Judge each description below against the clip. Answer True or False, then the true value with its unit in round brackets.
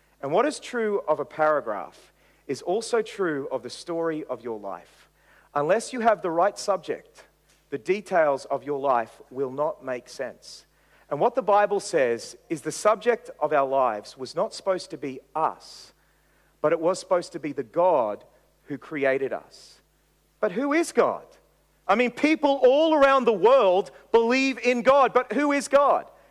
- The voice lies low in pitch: False (205 Hz)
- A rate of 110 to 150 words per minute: False (175 wpm)